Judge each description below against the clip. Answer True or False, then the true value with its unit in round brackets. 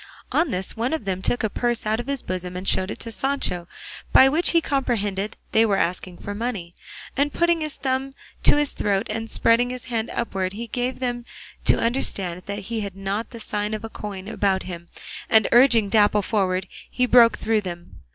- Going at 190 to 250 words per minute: True (205 wpm)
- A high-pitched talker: True (220 Hz)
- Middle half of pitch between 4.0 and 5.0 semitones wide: True (4.3 semitones)